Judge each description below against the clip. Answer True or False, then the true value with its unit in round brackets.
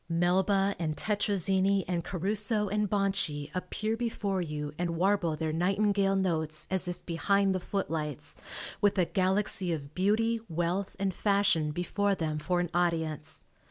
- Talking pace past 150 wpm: False (145 wpm)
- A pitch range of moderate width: True (3.4 semitones)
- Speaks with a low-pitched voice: False (185 Hz)